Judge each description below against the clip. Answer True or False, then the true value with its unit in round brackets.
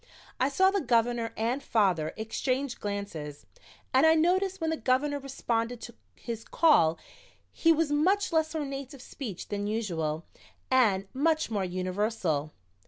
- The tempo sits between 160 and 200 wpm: False (145 wpm)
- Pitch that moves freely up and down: True (6.6 semitones)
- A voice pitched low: False (240 Hz)